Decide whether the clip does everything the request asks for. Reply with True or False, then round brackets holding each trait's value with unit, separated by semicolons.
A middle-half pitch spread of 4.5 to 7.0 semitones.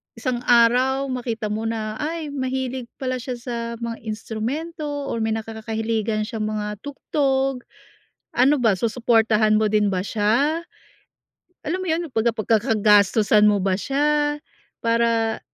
False (3.6 semitones)